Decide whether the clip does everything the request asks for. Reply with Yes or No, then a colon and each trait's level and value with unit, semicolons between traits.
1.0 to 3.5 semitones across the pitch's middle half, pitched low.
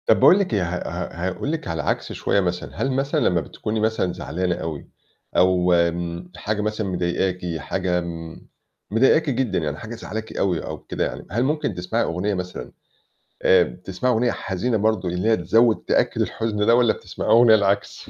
No: average, 4.1 semitones; very low, 95 Hz